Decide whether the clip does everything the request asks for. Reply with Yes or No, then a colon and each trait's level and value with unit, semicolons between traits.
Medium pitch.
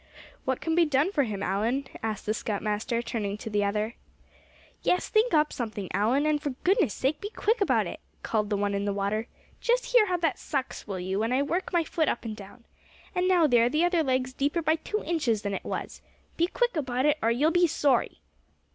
No: very high, 260 Hz